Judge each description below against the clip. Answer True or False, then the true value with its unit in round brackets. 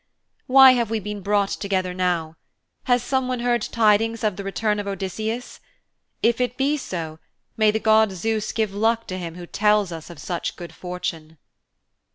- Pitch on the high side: True (210 Hz)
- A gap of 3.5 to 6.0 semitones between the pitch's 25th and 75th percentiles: True (3.9 semitones)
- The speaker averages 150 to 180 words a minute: True (175 wpm)